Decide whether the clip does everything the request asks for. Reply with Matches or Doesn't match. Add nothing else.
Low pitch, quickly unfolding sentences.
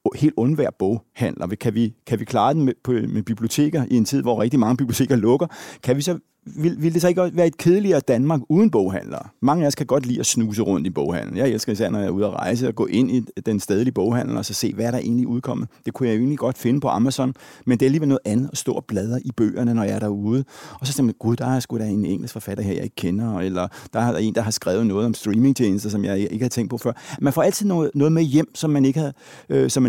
Matches